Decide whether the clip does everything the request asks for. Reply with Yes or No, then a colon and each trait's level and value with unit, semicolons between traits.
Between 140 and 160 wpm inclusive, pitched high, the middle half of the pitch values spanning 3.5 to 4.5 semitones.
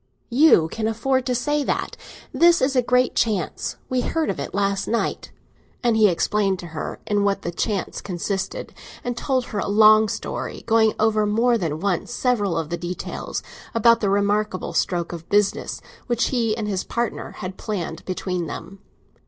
No: average, 175 wpm; high, 210 Hz; average, 3.8 semitones